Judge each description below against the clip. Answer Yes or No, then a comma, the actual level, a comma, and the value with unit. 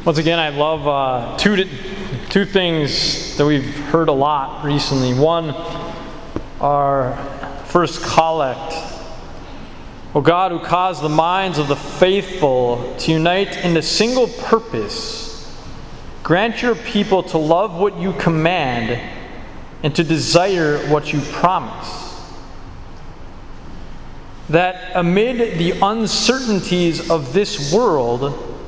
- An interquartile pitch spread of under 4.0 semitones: No, average, 4.3 semitones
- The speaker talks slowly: Yes, slow, 115 wpm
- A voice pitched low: No, medium, 165 Hz